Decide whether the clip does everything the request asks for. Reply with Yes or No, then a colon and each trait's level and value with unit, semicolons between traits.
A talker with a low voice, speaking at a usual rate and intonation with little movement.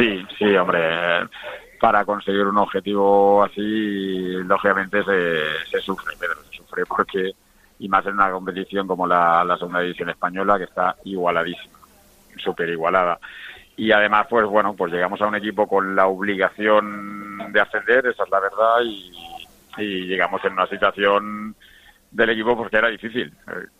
Yes: low, 100 Hz; average, 155 wpm; narrow, 1.8 semitones